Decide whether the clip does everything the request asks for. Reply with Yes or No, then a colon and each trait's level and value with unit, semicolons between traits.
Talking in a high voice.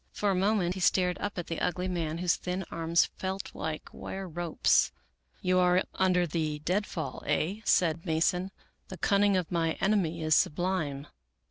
No: medium, 180 Hz